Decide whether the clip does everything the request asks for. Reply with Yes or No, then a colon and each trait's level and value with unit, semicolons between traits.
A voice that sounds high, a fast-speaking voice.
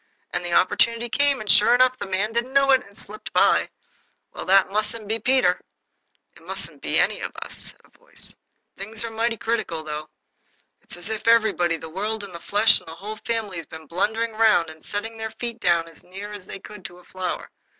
Yes: high, 210 Hz; fast, 220 wpm